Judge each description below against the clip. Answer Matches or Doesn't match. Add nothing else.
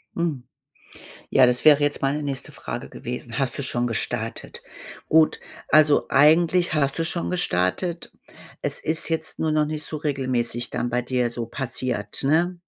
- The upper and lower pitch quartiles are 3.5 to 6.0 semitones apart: Matches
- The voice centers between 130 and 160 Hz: Matches